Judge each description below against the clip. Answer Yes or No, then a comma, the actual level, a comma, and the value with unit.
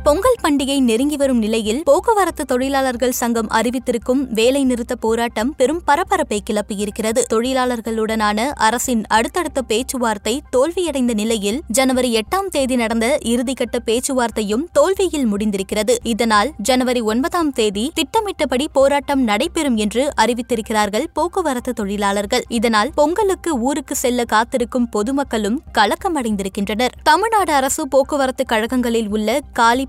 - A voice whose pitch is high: Yes, very high, 250 Hz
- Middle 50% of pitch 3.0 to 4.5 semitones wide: Yes, average, 4.1 semitones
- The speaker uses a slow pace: No, average, 105 wpm